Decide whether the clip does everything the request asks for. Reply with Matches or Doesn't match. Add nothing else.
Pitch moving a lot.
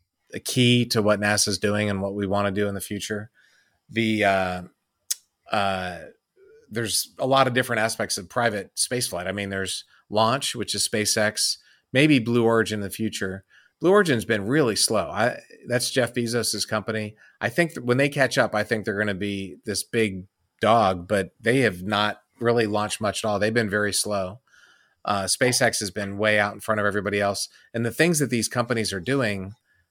Doesn't match